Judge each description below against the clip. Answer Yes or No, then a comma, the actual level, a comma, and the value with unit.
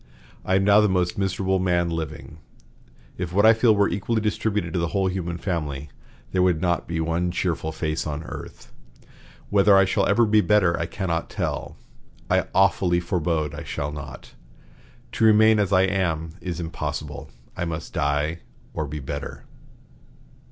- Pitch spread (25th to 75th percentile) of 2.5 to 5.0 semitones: Yes, average, 3.4 semitones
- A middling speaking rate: Yes, average, 165 wpm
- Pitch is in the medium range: No, very low, 90 Hz